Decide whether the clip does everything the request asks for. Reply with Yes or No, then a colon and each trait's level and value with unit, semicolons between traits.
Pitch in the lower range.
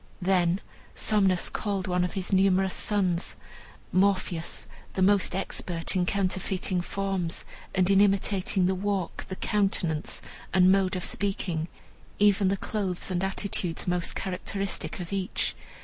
No: high, 190 Hz